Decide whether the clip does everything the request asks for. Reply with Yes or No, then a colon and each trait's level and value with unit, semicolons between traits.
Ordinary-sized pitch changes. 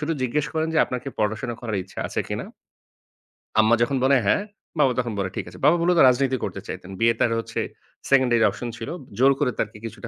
Yes: average, 3.6 semitones